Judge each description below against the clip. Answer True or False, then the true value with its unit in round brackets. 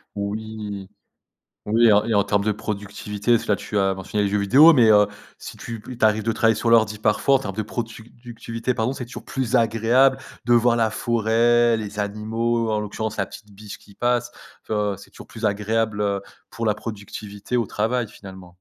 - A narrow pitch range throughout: True (2.2 semitones)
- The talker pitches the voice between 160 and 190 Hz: False (110 Hz)